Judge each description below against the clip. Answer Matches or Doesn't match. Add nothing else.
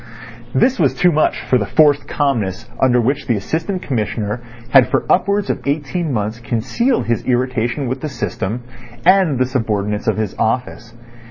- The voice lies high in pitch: Doesn't match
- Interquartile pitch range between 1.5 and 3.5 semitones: Doesn't match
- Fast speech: Doesn't match